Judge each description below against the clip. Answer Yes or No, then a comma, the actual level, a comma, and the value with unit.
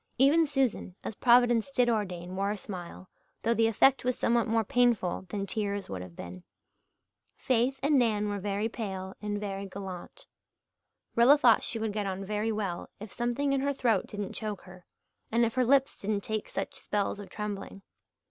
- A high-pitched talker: Yes, high, 215 Hz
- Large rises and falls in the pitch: No, average, 3.4 semitones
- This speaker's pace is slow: No, average, 185 wpm